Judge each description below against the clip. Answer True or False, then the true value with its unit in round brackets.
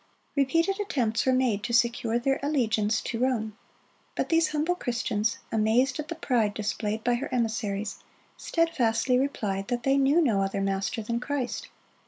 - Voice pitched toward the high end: True (240 Hz)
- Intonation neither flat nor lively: True (4.1 semitones)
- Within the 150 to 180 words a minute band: True (160 wpm)